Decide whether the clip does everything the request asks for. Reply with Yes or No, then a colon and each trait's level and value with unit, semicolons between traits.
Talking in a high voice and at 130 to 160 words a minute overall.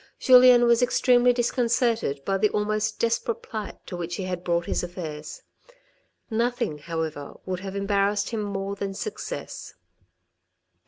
Yes: high, 205 Hz; average, 140 wpm